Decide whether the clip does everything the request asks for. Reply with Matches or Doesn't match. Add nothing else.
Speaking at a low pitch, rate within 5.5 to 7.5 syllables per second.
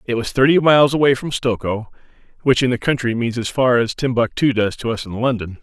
Matches